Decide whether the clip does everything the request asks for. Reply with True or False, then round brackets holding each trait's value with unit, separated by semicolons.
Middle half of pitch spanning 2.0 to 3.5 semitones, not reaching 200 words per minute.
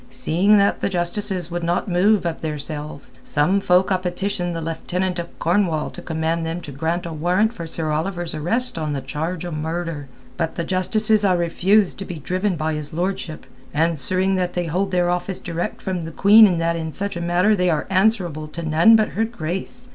False (2.9 semitones; 205 wpm)